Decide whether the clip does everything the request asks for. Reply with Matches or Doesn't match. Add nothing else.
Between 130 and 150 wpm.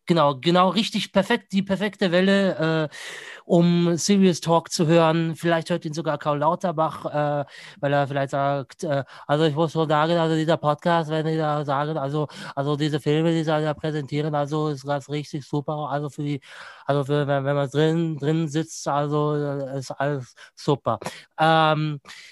Doesn't match